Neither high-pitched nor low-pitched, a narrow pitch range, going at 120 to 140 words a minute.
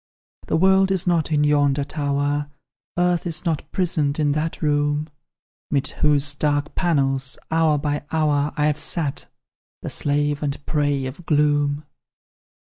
Yes: medium, 150 Hz; narrow, 1.8 semitones; slow, 135 wpm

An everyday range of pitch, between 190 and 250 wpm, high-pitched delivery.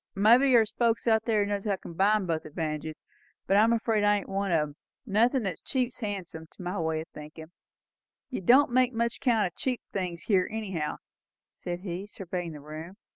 Yes: average, 4.9 semitones; average, 195 wpm; high, 195 Hz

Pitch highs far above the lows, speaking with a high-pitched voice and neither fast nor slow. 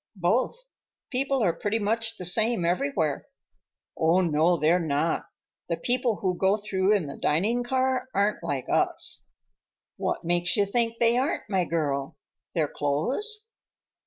Yes: wide, 6.3 semitones; high, 195 Hz; average, 145 wpm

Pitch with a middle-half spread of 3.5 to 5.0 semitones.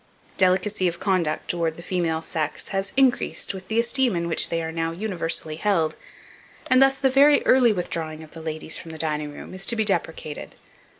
Yes: average, 4.7 semitones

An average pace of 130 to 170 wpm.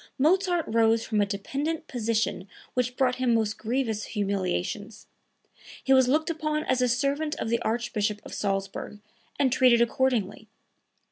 Yes: average, 145 wpm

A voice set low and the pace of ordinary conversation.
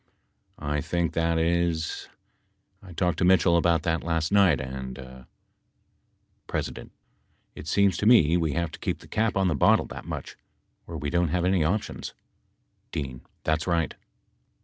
Yes: very low, 85 Hz; average, 165 wpm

